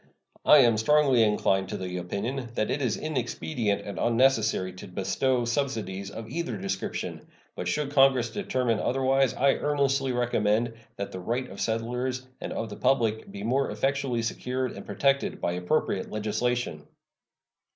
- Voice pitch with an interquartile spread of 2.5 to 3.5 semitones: No, average, 4.3 semitones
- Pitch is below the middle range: Yes, low, 120 Hz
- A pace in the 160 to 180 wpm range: No, average, 150 wpm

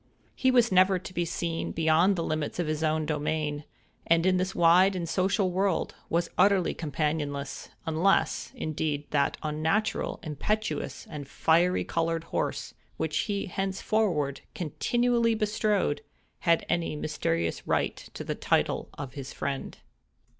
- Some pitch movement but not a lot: Yes, average, 4.0 semitones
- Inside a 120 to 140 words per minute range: Yes, slow, 135 wpm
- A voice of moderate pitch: Yes, medium, 165 Hz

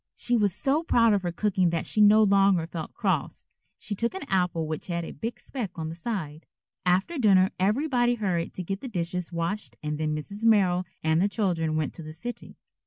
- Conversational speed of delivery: No, fast, 210 wpm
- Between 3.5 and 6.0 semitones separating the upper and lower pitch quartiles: Yes, average, 4.5 semitones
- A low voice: No, high, 190 Hz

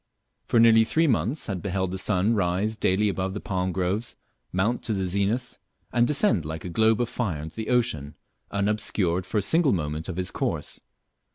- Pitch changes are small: No, average, 3.7 semitones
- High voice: No, low, 100 Hz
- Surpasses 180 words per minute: Yes, average, 190 wpm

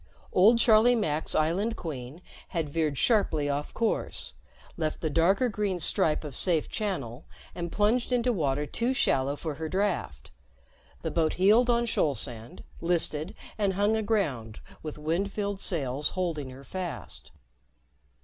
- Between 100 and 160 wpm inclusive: Yes, average, 145 wpm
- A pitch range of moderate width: No, wide, 5.9 semitones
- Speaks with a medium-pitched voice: Yes, medium, 170 Hz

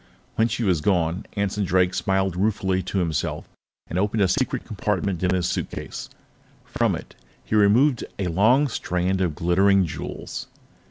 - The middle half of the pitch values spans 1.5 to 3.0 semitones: Yes, narrow, 2.4 semitones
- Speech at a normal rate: Yes, average, 155 wpm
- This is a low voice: Yes, very low, 95 Hz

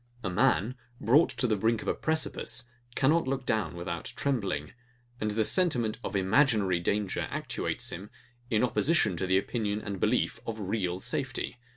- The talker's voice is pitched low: Yes, low, 110 Hz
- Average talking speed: Yes, average, 165 wpm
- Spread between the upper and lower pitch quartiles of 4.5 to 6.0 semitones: Yes, average, 4.9 semitones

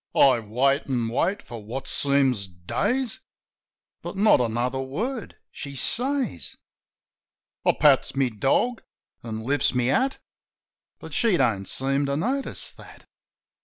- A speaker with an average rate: No, slow, 130 wpm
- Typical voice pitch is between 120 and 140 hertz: Yes, low, 135 Hz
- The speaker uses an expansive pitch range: Yes, wide, 8.5 semitones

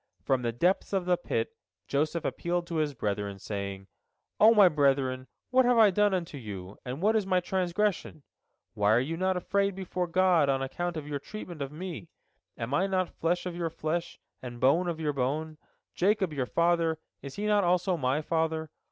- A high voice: No, medium, 165 Hz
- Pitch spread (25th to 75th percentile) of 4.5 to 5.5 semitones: Yes, average, 5.2 semitones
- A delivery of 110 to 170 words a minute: No, average, 195 wpm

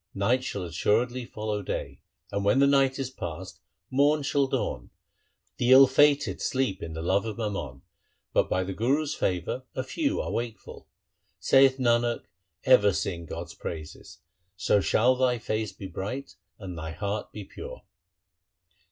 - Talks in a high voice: No, low, 110 Hz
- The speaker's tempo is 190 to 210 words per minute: No, average, 155 wpm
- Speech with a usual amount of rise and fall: No, wide, 5.7 semitones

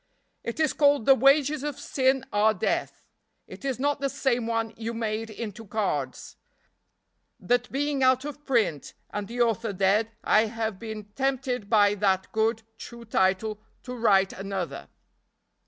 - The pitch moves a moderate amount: Yes, average, 4.0 semitones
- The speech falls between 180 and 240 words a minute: No, average, 155 wpm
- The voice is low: No, high, 225 Hz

